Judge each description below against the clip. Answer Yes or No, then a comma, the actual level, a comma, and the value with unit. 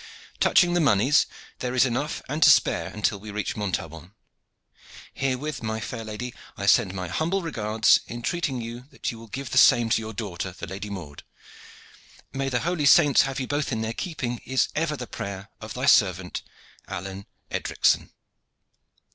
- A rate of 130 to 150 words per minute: No, average, 170 wpm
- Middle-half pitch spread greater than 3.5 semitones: Yes, average, 4.9 semitones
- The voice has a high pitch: No, low, 115 Hz